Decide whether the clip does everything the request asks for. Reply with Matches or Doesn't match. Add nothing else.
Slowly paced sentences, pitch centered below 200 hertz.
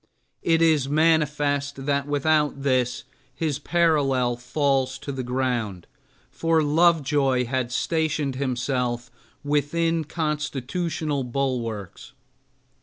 Matches